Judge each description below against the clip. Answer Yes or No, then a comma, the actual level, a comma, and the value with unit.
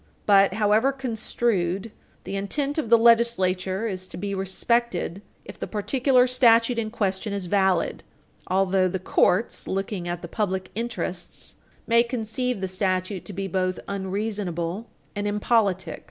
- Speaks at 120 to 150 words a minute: Yes, average, 140 wpm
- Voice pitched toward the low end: No, high, 200 Hz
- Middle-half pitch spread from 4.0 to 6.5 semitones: No, average, 3.6 semitones